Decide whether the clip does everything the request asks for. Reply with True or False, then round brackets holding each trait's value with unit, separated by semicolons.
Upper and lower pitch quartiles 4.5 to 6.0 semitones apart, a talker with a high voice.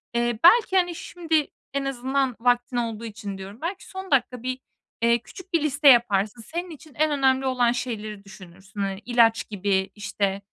True (5.4 semitones; 245 Hz)